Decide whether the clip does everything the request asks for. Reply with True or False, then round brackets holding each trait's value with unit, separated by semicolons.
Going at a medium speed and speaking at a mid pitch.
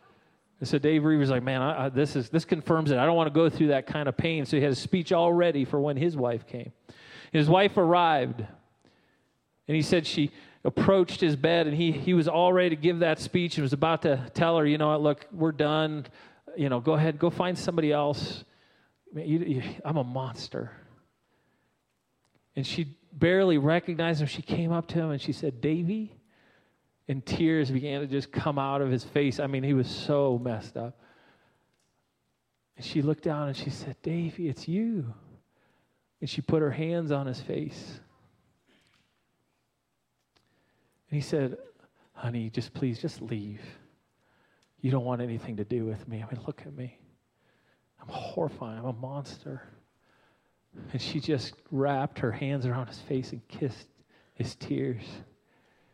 True (180 wpm; 150 Hz)